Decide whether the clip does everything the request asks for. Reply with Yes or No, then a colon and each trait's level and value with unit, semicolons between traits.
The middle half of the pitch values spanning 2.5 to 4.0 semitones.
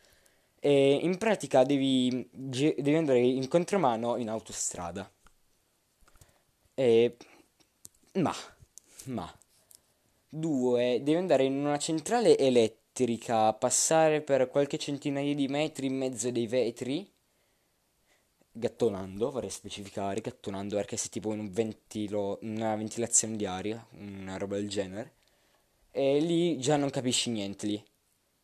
No: average, 4.8 semitones